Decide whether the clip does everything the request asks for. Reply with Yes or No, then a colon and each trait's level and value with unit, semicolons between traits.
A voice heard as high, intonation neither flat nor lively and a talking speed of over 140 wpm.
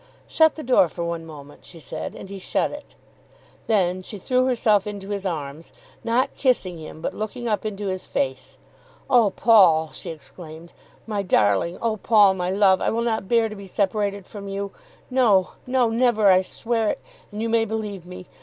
Yes: high, 200 Hz; average, 3.9 semitones; average, 190 wpm